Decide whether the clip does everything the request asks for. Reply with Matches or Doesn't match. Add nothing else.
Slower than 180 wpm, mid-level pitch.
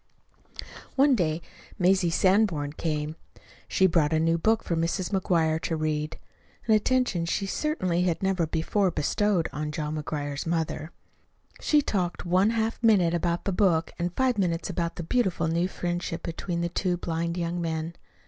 Matches